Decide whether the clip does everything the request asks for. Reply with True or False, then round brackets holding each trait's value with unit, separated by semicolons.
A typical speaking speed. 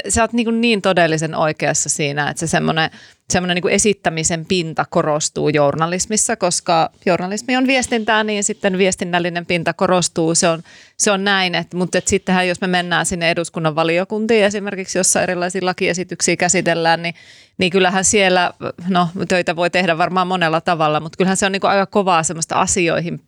False (170 wpm)